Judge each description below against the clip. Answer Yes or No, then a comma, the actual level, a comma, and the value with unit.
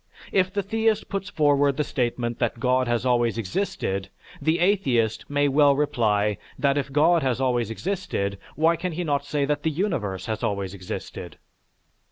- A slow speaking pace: No, average, 170 wpm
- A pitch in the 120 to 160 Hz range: Yes, medium, 140 Hz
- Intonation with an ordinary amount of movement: No, wide, 5.7 semitones